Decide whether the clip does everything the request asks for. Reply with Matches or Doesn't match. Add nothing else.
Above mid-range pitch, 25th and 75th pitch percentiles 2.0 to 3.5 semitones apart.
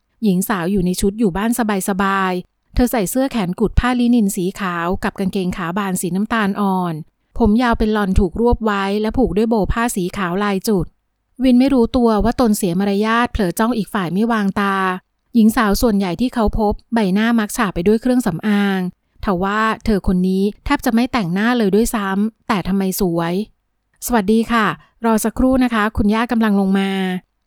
Matches